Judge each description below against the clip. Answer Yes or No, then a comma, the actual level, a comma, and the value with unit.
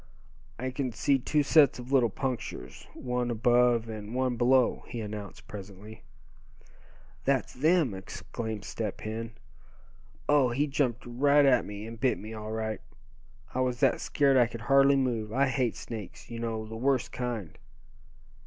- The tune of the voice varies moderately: Yes, average, 3.2 semitones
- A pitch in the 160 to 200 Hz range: No, low, 120 Hz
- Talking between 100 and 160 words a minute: Yes, average, 155 wpm